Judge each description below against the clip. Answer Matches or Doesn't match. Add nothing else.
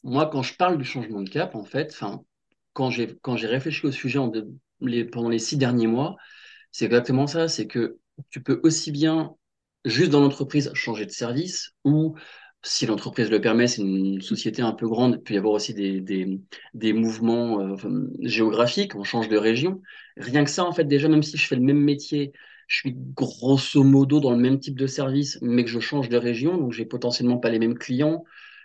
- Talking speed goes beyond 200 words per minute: Matches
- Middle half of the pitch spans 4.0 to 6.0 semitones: Matches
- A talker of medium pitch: Doesn't match